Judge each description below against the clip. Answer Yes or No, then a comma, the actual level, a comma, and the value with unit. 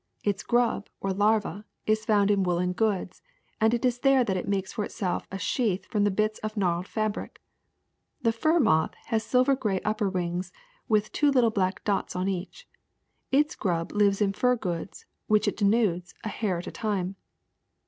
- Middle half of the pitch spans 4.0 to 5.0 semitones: No, average, 3.0 semitones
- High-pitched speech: Yes, high, 205 Hz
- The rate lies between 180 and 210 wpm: Yes, average, 190 wpm